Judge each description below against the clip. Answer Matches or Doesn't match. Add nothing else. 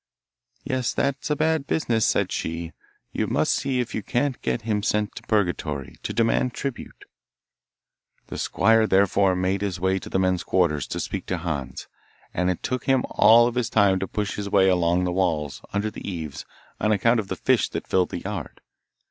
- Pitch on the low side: Matches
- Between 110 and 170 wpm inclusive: Doesn't match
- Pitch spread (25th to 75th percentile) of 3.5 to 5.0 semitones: Matches